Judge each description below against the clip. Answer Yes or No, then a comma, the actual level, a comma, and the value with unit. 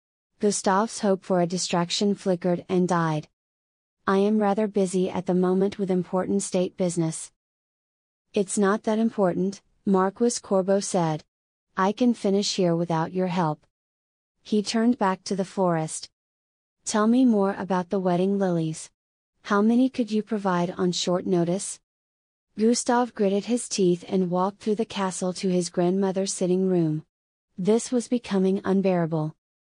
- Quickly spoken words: No, average, 145 wpm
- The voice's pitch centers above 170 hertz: Yes, high, 190 Hz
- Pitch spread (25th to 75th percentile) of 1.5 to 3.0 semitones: Yes, narrow, 2.6 semitones